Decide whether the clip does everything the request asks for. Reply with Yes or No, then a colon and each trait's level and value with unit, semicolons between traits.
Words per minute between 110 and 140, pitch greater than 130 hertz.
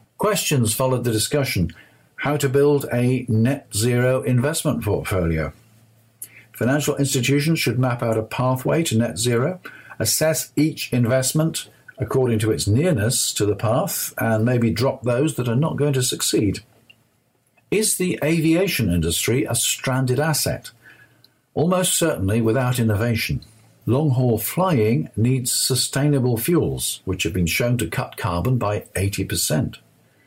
No: slow, 135 wpm; low, 125 Hz